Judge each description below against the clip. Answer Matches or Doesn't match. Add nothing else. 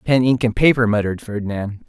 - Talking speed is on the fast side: Doesn't match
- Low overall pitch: Matches